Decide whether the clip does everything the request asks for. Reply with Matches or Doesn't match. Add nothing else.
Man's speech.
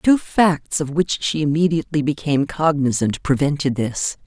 Doesn't match